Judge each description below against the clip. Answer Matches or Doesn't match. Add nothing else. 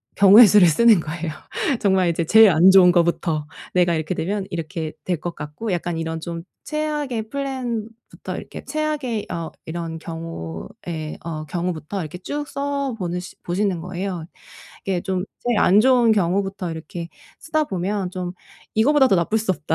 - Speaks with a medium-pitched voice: Matches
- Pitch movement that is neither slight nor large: Matches